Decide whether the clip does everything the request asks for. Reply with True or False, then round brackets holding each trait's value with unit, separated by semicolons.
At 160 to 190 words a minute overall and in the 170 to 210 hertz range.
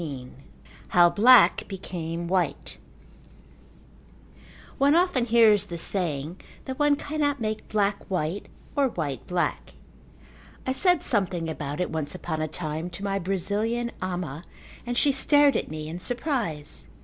False (135 wpm; 190 Hz)